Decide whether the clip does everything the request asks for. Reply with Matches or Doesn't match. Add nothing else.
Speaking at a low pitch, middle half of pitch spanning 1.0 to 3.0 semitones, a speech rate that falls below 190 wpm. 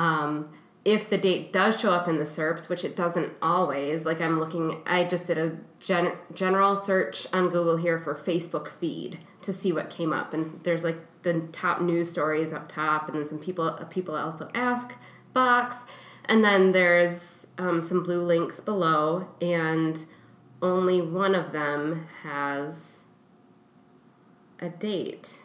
Doesn't match